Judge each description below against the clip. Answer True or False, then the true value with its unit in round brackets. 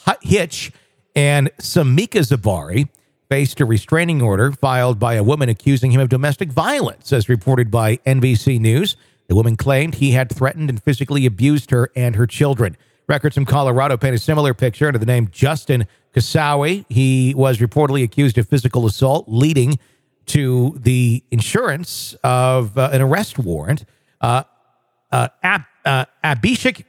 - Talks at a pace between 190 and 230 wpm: False (150 wpm)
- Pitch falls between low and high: False (130 Hz)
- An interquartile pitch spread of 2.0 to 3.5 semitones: True (2.6 semitones)